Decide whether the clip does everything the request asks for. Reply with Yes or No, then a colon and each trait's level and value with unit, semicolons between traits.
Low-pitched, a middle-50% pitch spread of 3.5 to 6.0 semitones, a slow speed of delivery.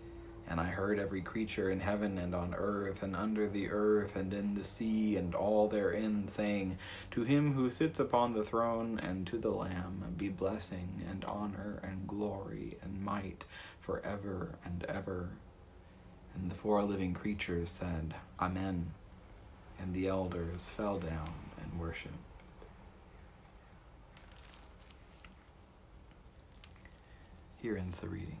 No: very low, 95 Hz; narrow, 2.6 semitones; slow, 130 wpm